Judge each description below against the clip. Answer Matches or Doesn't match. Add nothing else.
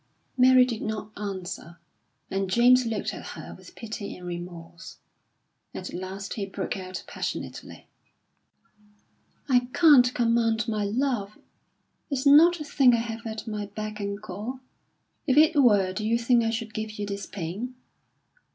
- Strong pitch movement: Doesn't match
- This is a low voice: Doesn't match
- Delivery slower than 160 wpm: Matches